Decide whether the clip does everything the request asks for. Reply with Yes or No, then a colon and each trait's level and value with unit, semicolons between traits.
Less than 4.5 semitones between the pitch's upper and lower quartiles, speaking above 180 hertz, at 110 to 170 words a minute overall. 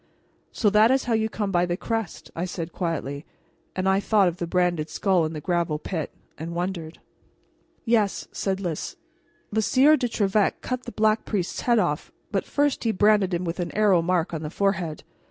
No: average, 4.1 semitones; high, 190 Hz; average, 195 wpm